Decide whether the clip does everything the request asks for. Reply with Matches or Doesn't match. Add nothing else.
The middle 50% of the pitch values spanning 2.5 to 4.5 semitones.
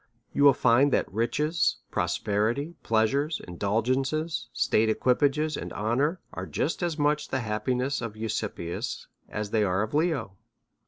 Doesn't match